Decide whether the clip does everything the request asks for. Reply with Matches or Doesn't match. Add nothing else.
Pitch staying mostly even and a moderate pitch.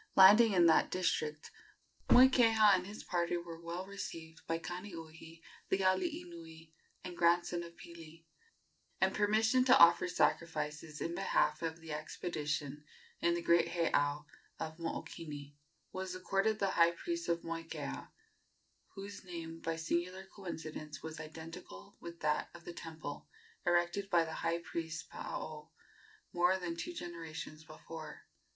Matches